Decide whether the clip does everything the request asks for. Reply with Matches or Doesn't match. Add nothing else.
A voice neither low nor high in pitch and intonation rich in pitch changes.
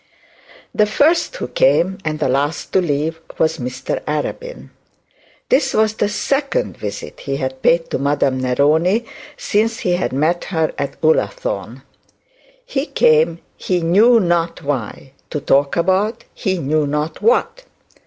Matches